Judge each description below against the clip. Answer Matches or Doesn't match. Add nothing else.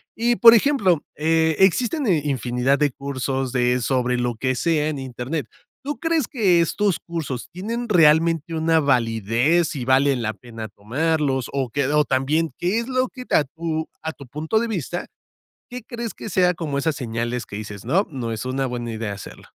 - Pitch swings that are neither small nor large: Doesn't match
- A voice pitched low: Doesn't match